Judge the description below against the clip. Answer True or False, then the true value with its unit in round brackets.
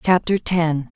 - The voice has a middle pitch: True (170 Hz)